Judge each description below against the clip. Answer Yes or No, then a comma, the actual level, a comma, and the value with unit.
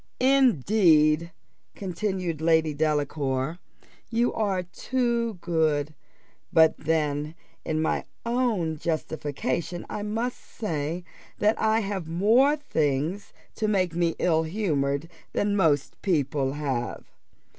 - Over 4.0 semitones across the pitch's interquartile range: Yes, wide, 5.4 semitones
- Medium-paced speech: No, slow, 105 wpm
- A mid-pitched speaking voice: Yes, medium, 165 Hz